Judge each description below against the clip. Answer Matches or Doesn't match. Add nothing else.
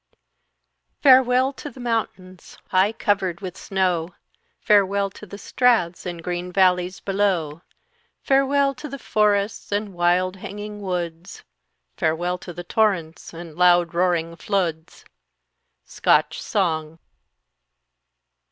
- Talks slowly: Matches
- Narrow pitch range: Doesn't match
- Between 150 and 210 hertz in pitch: Matches